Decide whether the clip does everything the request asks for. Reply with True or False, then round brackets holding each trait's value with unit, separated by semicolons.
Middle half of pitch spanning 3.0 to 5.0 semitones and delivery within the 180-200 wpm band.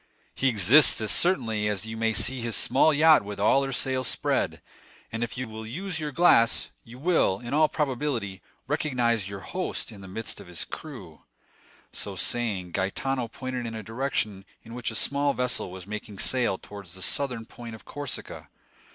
True (4.4 semitones; 185 wpm)